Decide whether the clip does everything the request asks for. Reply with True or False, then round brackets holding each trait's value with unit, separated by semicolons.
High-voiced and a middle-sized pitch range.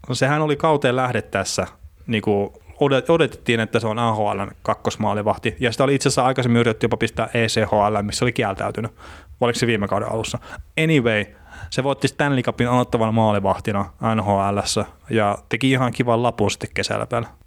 False (115 Hz; 3.5 semitones)